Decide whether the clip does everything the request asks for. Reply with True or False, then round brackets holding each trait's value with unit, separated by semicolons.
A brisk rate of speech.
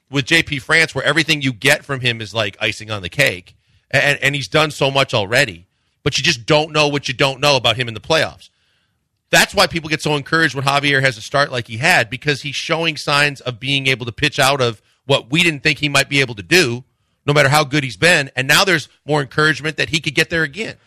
True (255 wpm)